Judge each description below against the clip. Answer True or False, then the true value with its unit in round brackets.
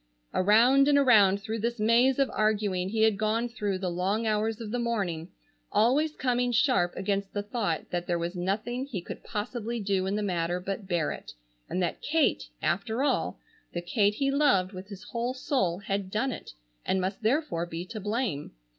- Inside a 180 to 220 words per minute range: True (190 wpm)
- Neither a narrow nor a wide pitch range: True (4.3 semitones)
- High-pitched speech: True (210 Hz)